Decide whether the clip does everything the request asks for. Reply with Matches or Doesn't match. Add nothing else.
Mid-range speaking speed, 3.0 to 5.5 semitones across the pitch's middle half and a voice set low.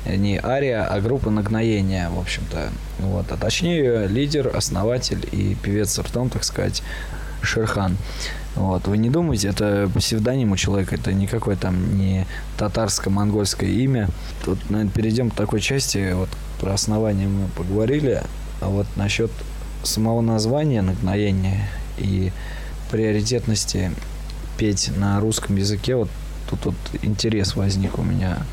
Doesn't match